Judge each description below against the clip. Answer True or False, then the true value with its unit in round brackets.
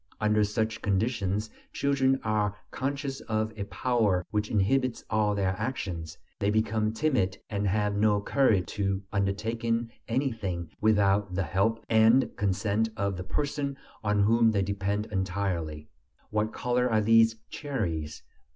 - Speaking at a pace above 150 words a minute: False (135 wpm)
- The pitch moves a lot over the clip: False (2.5 semitones)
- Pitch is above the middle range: False (105 Hz)